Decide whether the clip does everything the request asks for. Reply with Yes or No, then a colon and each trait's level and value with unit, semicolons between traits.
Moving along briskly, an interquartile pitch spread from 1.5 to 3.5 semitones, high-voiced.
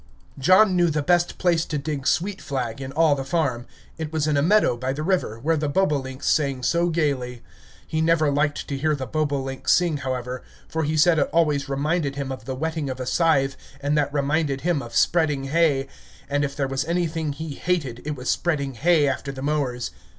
No: fast, 210 wpm; average, 3.2 semitones; medium, 145 Hz